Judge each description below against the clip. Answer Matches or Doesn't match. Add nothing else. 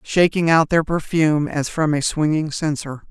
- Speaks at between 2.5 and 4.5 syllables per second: Matches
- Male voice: Doesn't match